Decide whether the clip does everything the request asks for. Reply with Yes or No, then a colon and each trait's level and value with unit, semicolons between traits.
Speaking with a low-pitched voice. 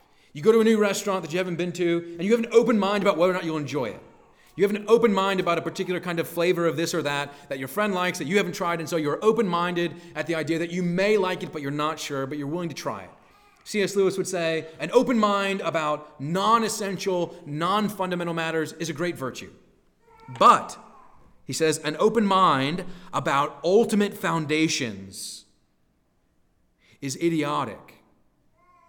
No: medium, 175 Hz